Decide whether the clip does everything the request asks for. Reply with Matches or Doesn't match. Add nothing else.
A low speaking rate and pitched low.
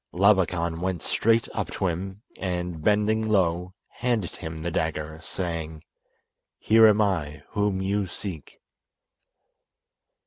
Matches